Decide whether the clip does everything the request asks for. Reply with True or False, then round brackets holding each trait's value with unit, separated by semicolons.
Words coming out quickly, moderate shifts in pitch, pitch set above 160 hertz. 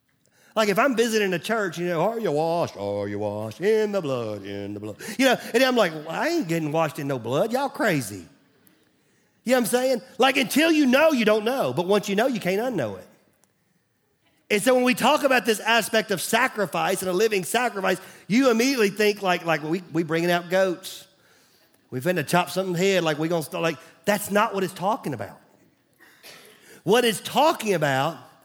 False (210 wpm; 5.9 semitones; 190 Hz)